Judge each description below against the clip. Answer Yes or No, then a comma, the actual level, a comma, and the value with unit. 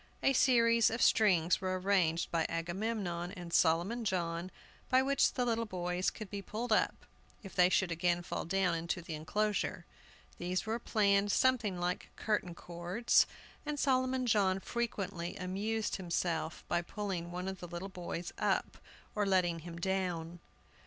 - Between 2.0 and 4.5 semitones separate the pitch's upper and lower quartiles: Yes, average, 3.9 semitones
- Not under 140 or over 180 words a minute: Yes, average, 155 wpm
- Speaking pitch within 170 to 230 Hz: Yes, medium, 185 Hz